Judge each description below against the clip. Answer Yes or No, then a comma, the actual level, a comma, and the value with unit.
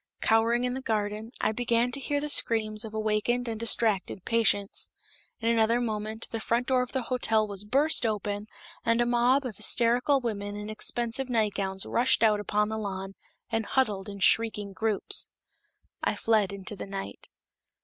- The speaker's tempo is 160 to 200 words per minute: Yes, average, 170 wpm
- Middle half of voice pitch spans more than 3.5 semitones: No, narrow, 2.5 semitones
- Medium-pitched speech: No, high, 220 Hz